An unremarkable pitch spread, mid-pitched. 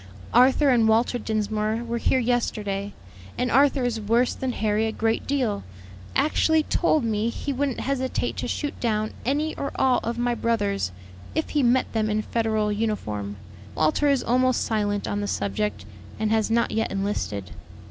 No: average, 3.3 semitones; high, 225 Hz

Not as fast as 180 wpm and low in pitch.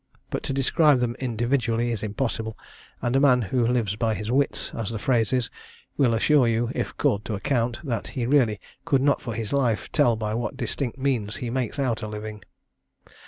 No: average, 200 wpm; low, 120 Hz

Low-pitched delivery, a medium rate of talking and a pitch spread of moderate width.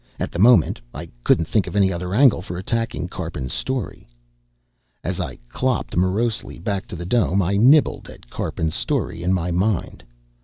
Yes: very low, 95 Hz; average, 175 wpm; average, 4.7 semitones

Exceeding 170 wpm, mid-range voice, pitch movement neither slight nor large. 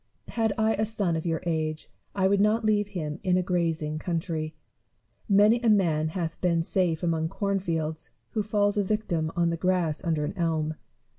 Yes: average, 180 wpm; medium, 175 Hz; average, 4.1 semitones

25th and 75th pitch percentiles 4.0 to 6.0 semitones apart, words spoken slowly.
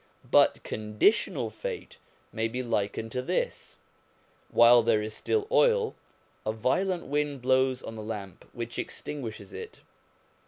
Yes: average, 5.1 semitones; slow, 130 wpm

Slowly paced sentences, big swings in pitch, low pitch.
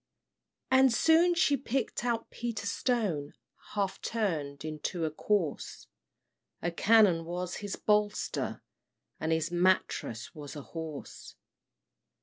No: slow, 115 wpm; wide, 6.0 semitones; high, 190 Hz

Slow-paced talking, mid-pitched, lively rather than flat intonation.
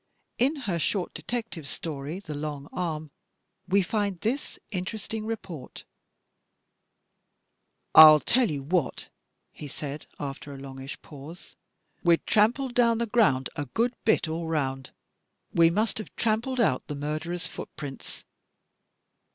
Yes: slow, 130 wpm; medium, 170 Hz; wide, 7.0 semitones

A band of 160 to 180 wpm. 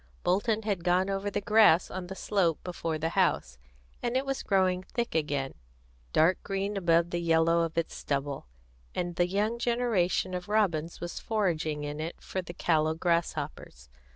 Yes: average, 170 wpm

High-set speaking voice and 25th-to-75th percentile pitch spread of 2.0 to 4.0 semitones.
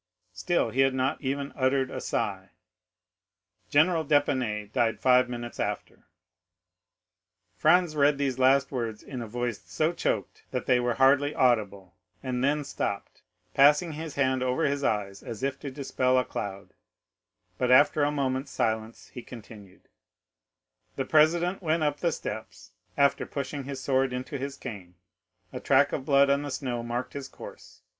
No: low, 130 Hz; average, 3.0 semitones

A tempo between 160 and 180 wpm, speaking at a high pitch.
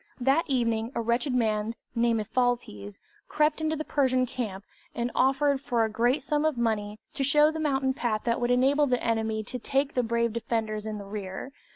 No: average, 195 wpm; high, 240 Hz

